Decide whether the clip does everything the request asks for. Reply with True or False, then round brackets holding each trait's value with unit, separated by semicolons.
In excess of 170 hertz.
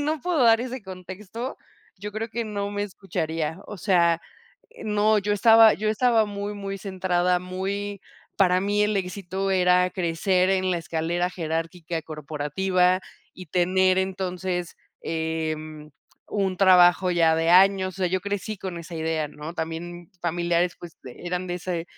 True (185 Hz)